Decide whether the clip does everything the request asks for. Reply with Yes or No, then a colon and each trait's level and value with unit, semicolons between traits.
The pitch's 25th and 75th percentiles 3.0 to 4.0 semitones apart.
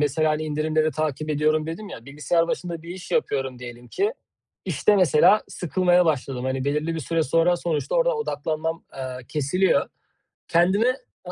Yes: average, 3.4 semitones